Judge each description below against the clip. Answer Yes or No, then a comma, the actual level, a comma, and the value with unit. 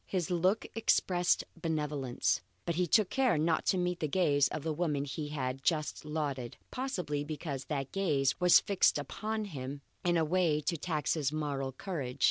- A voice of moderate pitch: Yes, medium, 155 Hz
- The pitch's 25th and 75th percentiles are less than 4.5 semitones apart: Yes, average, 3.9 semitones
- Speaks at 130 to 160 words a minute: No, average, 175 wpm